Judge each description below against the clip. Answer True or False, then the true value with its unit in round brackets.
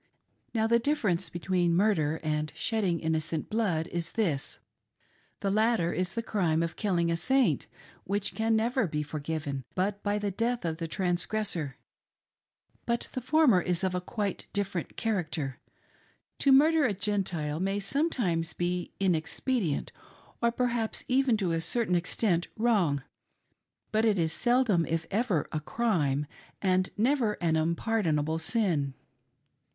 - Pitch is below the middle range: False (185 Hz)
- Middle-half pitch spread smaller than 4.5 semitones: False (5.4 semitones)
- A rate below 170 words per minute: True (145 wpm)